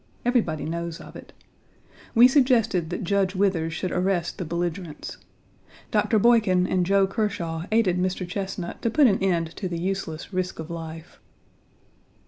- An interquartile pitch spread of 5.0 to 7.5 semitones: No, average, 3.1 semitones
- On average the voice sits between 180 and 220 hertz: Yes, medium, 185 Hz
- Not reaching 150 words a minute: No, average, 155 wpm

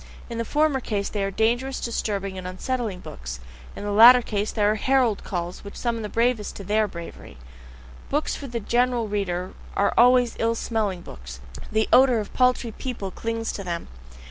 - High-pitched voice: Yes, high, 220 Hz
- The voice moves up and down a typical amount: Yes, average, 3.6 semitones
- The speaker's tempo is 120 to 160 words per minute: No, average, 180 wpm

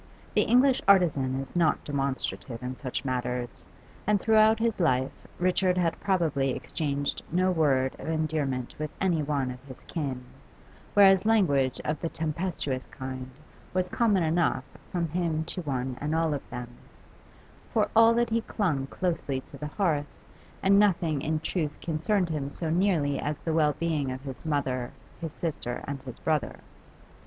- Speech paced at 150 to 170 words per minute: Yes, average, 160 wpm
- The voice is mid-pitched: Yes, medium, 155 Hz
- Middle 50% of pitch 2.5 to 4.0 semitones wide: No, average, 4.9 semitones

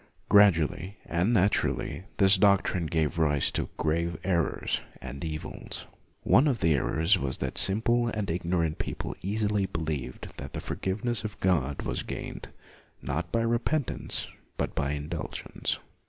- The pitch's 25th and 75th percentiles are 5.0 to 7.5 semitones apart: No, average, 4.6 semitones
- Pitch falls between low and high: No, very low, 90 Hz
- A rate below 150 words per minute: Yes, average, 140 wpm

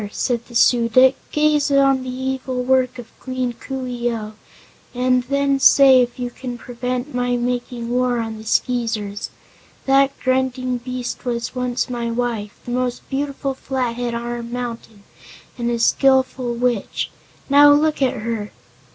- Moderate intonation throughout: No, narrow, 1.7 semitones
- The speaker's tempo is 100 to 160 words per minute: Yes, average, 155 wpm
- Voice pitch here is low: No, very high, 250 Hz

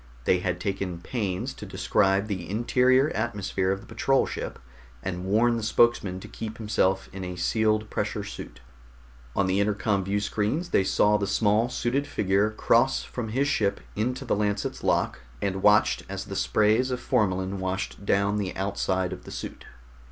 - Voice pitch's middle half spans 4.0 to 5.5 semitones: No, average, 2.9 semitones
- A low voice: Yes, low, 105 Hz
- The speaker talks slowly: No, average, 170 wpm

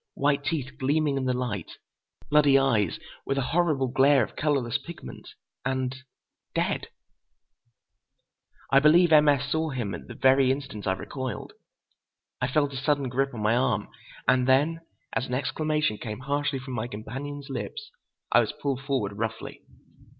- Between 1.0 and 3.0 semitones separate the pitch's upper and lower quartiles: Yes, narrow, 2.4 semitones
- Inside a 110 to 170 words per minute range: Yes, average, 155 wpm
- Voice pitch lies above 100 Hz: Yes, low, 135 Hz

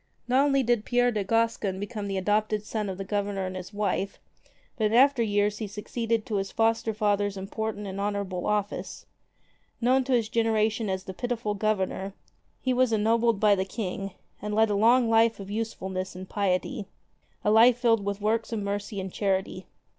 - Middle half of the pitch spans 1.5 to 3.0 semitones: Yes, narrow, 2.4 semitones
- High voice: Yes, high, 210 Hz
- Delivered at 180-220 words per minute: Yes, average, 185 wpm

